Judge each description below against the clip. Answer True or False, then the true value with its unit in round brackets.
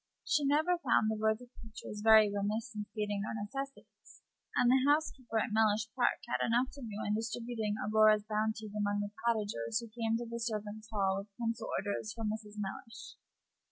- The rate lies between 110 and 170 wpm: False (180 wpm)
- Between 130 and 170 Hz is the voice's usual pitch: False (220 Hz)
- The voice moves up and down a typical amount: False (1.9 semitones)